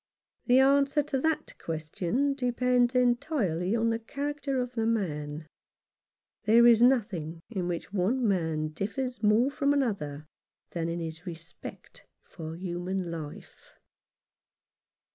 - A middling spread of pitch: No, wide, 7.0 semitones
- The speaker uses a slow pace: Yes, slow, 125 wpm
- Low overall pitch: No, high, 215 Hz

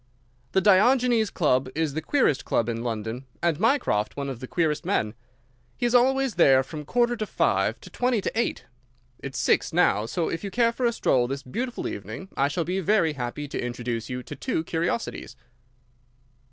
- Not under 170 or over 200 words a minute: Yes, average, 185 wpm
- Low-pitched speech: No, medium, 160 Hz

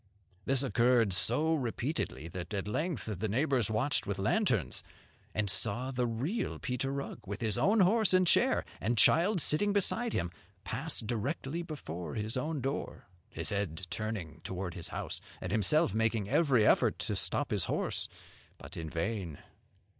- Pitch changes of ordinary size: No, wide, 7.0 semitones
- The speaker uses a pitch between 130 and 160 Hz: No, low, 115 Hz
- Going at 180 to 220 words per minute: No, average, 160 wpm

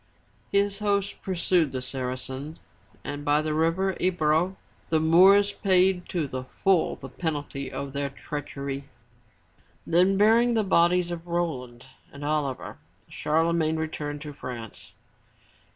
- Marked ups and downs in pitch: No, average, 4.6 semitones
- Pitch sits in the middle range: Yes, medium, 160 Hz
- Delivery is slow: Yes, slow, 130 wpm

